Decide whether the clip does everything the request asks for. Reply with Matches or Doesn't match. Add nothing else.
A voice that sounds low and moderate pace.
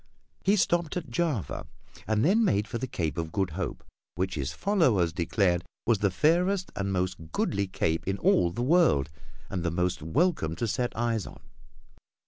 Matches